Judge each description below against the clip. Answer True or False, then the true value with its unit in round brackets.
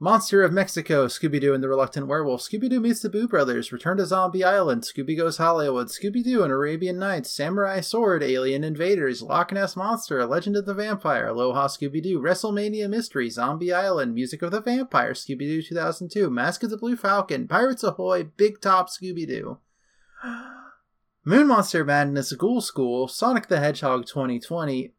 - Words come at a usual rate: True (175 wpm)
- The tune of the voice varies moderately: False (6.2 semitones)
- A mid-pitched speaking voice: True (180 Hz)